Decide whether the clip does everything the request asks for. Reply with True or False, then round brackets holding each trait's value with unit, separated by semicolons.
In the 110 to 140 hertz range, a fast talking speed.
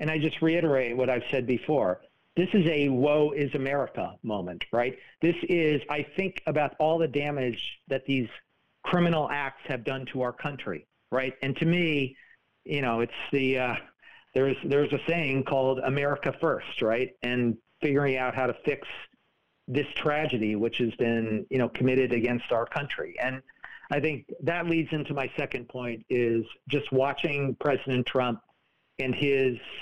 False (135 Hz; 165 wpm)